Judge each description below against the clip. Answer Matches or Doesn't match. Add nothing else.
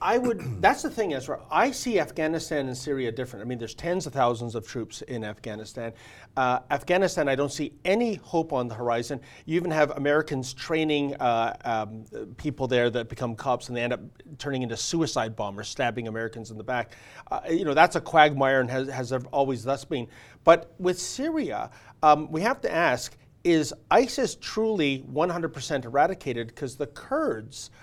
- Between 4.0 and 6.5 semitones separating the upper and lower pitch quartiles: Matches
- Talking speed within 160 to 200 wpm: Matches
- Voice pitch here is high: Doesn't match